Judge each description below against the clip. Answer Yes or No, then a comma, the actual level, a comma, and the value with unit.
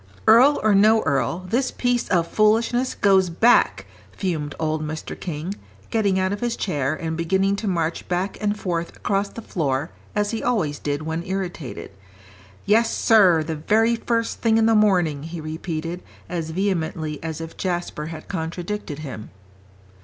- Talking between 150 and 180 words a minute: Yes, average, 160 wpm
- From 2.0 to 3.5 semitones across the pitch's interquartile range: No, average, 4.8 semitones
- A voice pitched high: No, medium, 180 Hz